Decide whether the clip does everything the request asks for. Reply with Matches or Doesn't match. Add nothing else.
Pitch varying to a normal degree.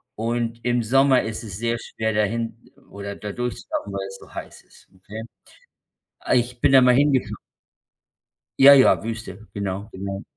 Matches